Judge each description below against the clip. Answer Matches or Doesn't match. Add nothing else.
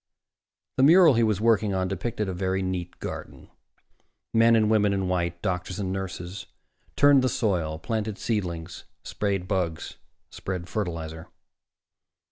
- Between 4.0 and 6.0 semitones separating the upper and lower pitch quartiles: Doesn't match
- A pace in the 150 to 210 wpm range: Doesn't match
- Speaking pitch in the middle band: Doesn't match